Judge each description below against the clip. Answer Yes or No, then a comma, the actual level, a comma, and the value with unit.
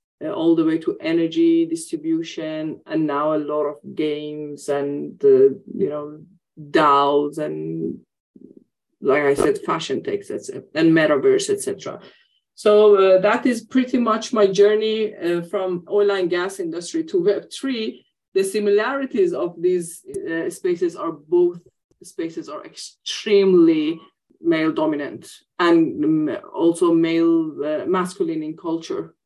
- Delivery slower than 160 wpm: Yes, slow, 135 wpm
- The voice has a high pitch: Yes, very high, 310 Hz